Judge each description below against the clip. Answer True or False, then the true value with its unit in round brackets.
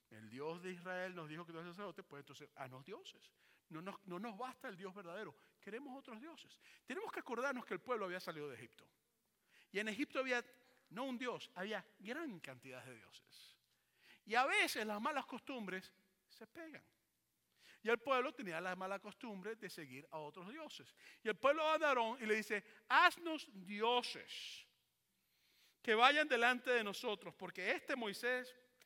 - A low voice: False (220 Hz)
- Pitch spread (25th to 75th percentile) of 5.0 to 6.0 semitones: True (5.6 semitones)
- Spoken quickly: False (180 wpm)